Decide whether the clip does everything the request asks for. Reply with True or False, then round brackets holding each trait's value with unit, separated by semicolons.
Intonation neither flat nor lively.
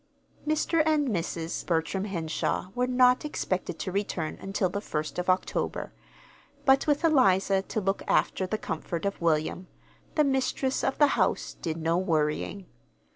False (7.2 semitones)